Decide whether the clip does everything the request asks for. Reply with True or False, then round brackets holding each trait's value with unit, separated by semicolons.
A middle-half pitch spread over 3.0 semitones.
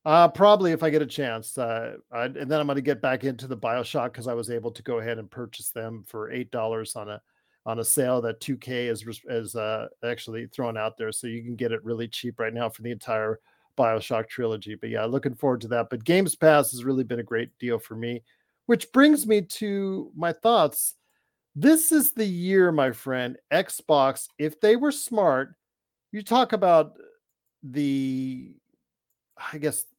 True (5.5 semitones)